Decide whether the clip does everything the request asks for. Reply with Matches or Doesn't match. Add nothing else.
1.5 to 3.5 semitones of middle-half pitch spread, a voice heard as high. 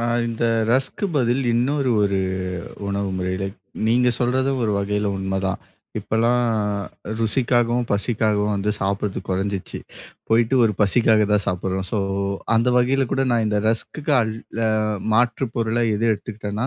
Doesn't match